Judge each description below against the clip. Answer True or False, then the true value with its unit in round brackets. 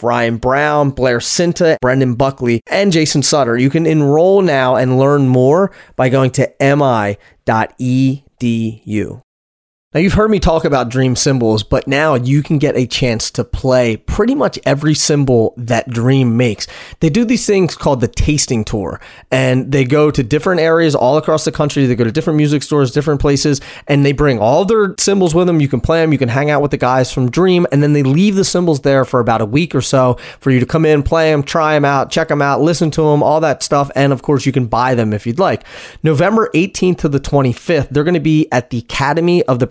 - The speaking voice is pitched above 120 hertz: True (140 Hz)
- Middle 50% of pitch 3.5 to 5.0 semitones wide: True (3.8 semitones)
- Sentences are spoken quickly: True (220 wpm)